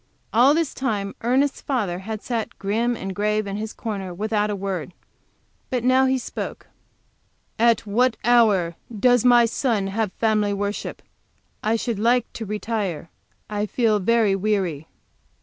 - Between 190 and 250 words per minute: No, average, 150 wpm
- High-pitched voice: Yes, high, 215 Hz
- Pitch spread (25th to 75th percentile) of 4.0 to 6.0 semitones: No, average, 3.0 semitones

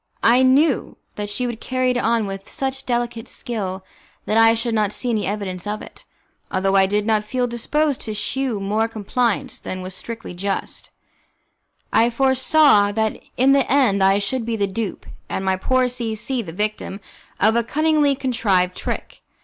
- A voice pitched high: Yes, high, 225 Hz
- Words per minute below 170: No, average, 180 wpm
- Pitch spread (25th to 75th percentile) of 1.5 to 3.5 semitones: No, average, 3.9 semitones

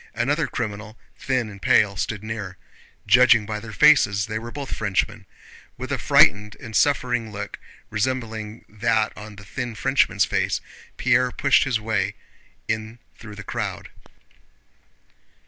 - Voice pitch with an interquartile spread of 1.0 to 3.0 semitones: Yes, narrow, 2.6 semitones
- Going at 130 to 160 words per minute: Yes, average, 140 wpm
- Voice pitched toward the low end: Yes, low, 110 Hz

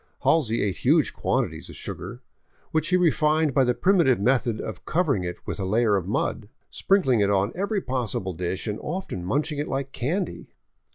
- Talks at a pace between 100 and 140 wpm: No, average, 195 wpm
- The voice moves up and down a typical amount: No, wide, 7.5 semitones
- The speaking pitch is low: Yes, low, 130 Hz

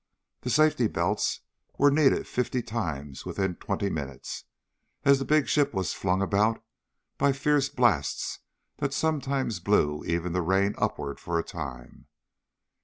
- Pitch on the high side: No, low, 105 Hz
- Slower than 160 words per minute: Yes, average, 140 wpm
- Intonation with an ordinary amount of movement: No, wide, 8.6 semitones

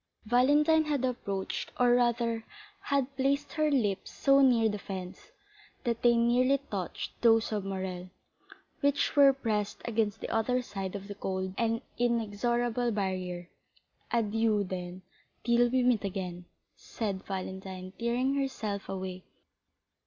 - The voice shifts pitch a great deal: No, average, 4.3 semitones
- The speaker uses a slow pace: Yes, slow, 130 wpm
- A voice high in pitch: Yes, high, 225 Hz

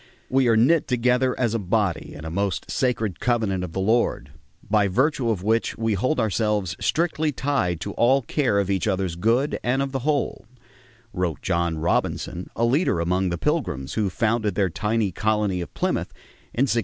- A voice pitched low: Yes, low, 110 Hz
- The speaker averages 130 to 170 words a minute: No, average, 185 wpm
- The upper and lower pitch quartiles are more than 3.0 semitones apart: Yes, average, 5.0 semitones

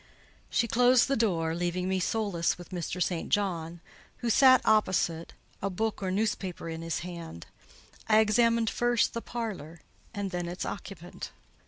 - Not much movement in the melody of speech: No, average, 4.5 semitones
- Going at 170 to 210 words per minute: No, average, 155 wpm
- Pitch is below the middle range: No, high, 190 Hz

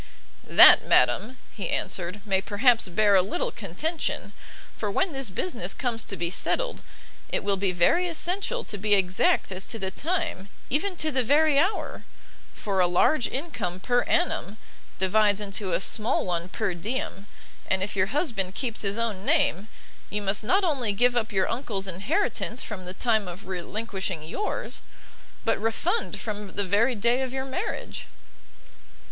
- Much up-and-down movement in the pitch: Yes, wide, 5.8 semitones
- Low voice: No, high, 210 Hz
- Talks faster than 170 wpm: No, average, 165 wpm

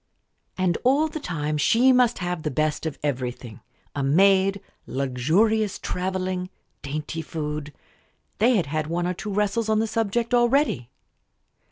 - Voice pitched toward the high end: No, medium, 180 Hz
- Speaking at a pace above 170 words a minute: No, average, 145 wpm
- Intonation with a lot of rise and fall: Yes, wide, 6.5 semitones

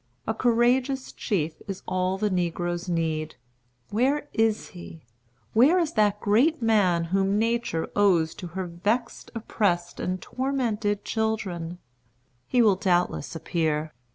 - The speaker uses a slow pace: Yes, slow, 125 wpm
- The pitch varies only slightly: No, average, 4.8 semitones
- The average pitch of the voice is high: Yes, high, 200 Hz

